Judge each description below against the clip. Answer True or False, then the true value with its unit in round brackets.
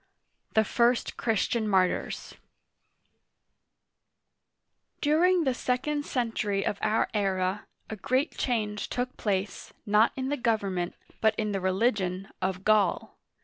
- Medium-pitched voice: False (215 Hz)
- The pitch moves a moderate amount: True (4.1 semitones)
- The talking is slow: True (115 wpm)